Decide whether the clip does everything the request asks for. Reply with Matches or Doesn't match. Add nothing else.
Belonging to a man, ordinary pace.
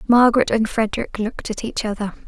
Doesn't match